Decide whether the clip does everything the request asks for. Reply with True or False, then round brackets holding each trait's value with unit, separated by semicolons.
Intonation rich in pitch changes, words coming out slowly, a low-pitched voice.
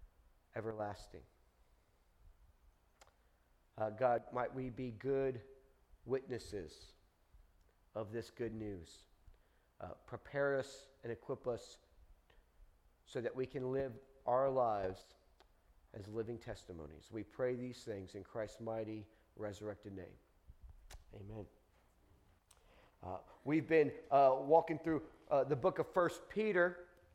True (7.2 semitones; 110 wpm; 110 Hz)